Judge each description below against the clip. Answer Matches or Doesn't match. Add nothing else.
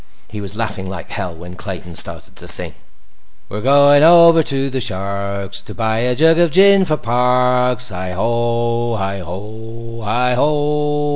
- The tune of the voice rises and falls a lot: Matches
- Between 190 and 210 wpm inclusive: Doesn't match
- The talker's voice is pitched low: Matches